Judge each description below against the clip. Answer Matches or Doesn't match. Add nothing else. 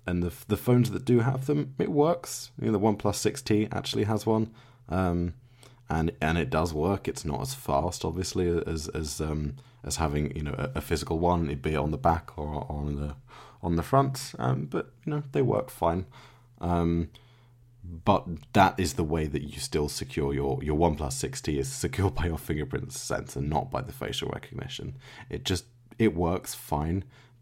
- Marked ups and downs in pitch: Matches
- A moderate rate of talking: Matches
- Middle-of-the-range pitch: Doesn't match